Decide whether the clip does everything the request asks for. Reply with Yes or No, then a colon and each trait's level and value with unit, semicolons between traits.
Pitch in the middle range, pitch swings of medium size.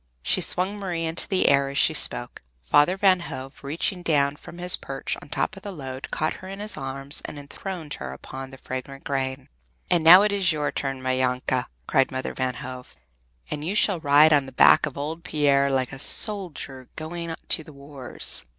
Yes: medium, 145 Hz; average, 4.4 semitones